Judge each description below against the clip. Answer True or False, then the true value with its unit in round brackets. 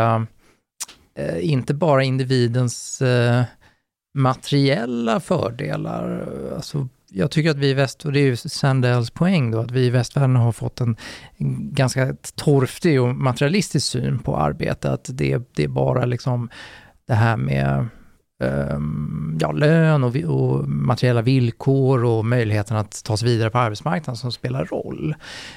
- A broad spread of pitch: False (3.6 semitones)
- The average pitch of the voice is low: True (125 Hz)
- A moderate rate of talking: True (145 wpm)